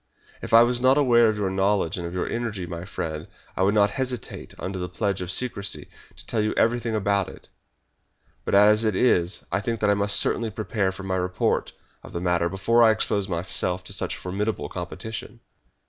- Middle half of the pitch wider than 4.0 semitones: No, average, 3.6 semitones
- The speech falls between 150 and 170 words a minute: No, fast, 205 wpm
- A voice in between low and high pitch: No, low, 100 Hz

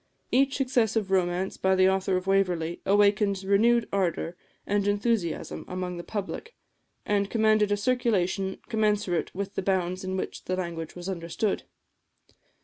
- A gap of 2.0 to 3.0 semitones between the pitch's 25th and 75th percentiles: Yes, narrow, 2.4 semitones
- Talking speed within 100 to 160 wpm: Yes, average, 145 wpm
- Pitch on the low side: No, high, 195 Hz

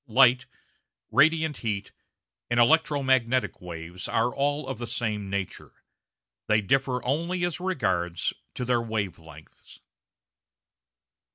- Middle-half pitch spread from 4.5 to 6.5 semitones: Yes, wide, 5.4 semitones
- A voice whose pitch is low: Yes, low, 120 Hz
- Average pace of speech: No, slow, 110 wpm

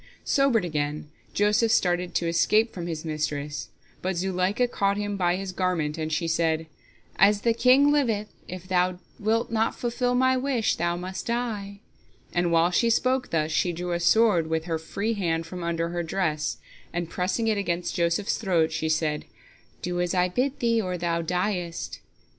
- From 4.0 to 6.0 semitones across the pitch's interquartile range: Yes, average, 4.3 semitones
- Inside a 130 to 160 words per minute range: No, average, 175 wpm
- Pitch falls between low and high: Yes, medium, 180 Hz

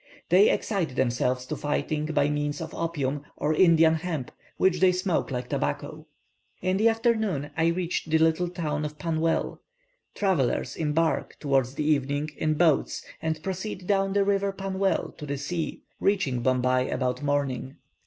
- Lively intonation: No, average, 4.3 semitones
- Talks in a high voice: No, medium, 160 Hz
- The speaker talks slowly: No, average, 155 wpm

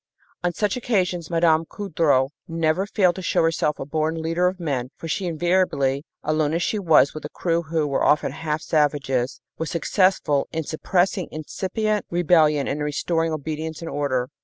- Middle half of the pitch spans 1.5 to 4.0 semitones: Yes, average, 2.9 semitones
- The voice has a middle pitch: Yes, medium, 160 Hz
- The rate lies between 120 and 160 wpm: No, average, 175 wpm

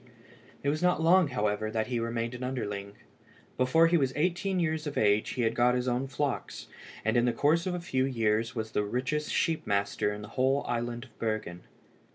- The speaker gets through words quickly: Yes, fast, 210 wpm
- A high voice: No, low, 125 Hz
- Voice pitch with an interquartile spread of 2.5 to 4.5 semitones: No, average, 5.2 semitones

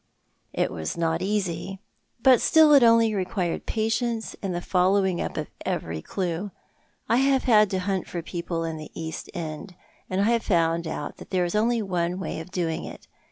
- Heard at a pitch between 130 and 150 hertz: No, medium, 185 Hz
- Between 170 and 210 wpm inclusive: Yes, average, 195 wpm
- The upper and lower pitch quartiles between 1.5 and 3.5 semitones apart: No, average, 4.3 semitones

